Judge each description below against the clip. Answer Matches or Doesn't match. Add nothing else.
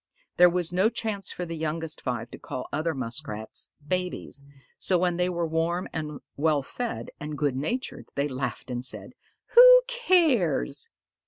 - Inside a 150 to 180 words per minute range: Matches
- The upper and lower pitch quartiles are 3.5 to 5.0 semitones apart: Matches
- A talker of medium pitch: Matches